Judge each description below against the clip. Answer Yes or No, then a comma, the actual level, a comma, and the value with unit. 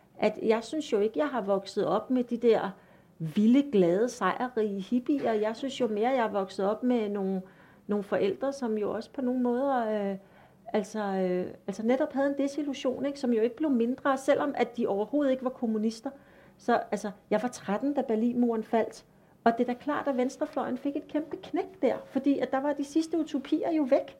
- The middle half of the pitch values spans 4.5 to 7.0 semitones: Yes, average, 4.8 semitones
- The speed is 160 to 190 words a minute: No, average, 215 wpm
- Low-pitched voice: No, high, 240 Hz